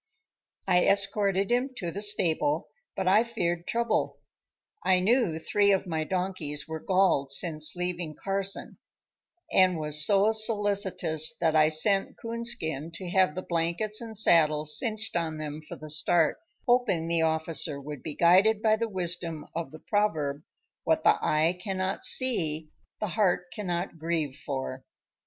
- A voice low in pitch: No, medium, 180 Hz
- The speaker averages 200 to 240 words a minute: No, average, 150 wpm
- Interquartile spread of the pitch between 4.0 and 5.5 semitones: Yes, average, 4.5 semitones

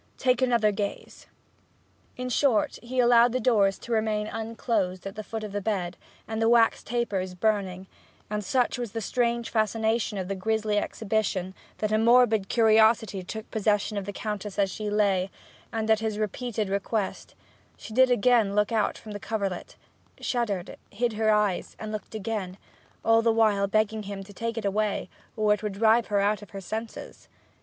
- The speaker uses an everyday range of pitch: No, narrow, 2.1 semitones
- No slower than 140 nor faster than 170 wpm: No, average, 180 wpm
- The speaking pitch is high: Yes, high, 215 Hz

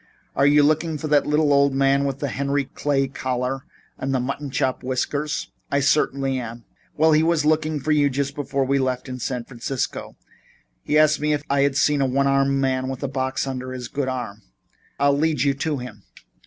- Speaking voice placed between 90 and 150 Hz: Yes, medium, 140 Hz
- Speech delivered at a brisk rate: Yes, fast, 210 wpm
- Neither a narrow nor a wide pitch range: No, narrow, 1.9 semitones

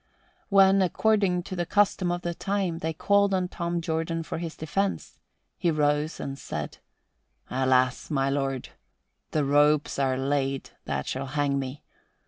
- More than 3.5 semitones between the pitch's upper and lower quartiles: Yes, average, 4.6 semitones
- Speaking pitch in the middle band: Yes, medium, 160 Hz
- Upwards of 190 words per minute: No, average, 150 wpm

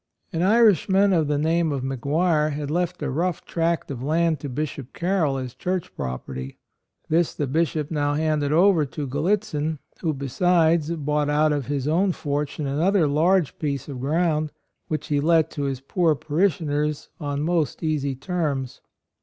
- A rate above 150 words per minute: Yes, average, 160 wpm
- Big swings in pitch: No, average, 2.9 semitones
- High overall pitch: No, medium, 155 Hz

